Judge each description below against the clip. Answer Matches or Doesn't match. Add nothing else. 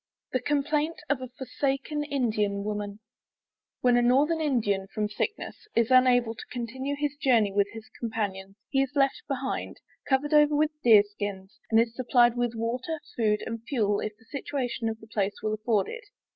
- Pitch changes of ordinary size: Matches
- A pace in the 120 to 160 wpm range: Doesn't match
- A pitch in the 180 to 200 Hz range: Doesn't match